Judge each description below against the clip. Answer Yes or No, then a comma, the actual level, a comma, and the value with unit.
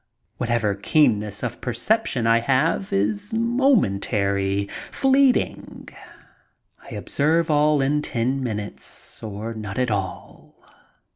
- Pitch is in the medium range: No, low, 120 Hz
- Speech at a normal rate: No, slow, 110 wpm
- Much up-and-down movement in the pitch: Yes, wide, 6.6 semitones